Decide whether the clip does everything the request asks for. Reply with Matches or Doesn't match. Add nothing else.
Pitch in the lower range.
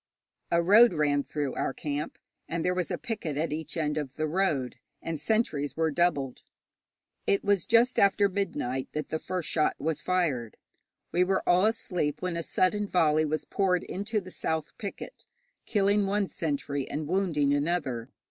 Doesn't match